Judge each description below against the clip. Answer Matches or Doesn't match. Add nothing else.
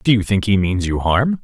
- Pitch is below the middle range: Matches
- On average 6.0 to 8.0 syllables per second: Doesn't match